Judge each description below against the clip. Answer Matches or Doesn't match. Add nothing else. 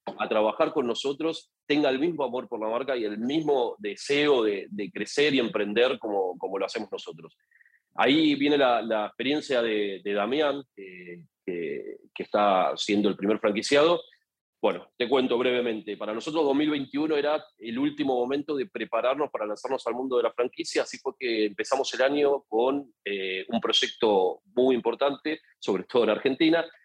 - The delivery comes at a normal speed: Matches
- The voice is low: Doesn't match